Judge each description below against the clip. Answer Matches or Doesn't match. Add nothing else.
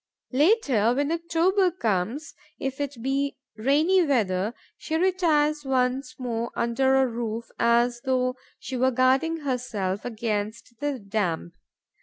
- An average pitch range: Matches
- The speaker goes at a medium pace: Doesn't match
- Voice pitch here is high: Matches